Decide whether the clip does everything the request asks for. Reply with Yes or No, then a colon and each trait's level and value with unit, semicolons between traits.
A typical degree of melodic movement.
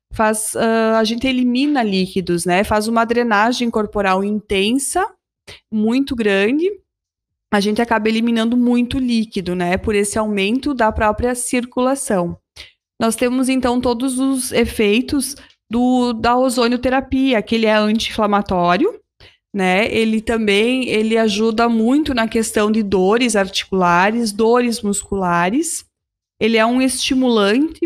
Yes: average, 3.0 semitones